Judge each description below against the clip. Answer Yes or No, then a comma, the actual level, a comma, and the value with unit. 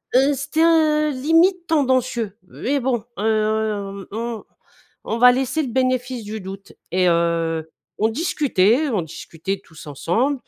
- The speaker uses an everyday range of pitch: No, wide, 5.9 semitones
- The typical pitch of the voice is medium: No, high, 235 Hz